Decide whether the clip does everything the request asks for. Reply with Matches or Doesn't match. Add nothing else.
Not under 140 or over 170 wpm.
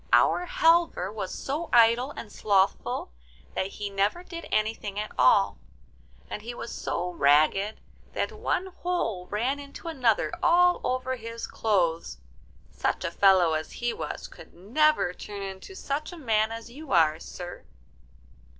Matches